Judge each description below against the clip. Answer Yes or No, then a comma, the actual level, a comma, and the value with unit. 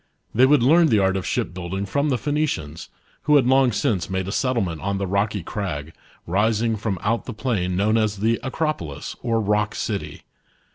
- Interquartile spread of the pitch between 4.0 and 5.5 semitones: Yes, average, 4.7 semitones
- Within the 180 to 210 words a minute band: Yes, average, 185 wpm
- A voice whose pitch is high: No, low, 105 Hz